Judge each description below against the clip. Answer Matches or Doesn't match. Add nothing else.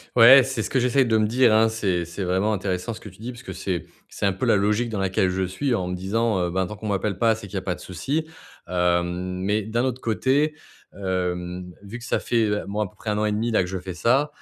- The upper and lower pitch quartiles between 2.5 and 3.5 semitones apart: Doesn't match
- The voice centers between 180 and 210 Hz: Doesn't match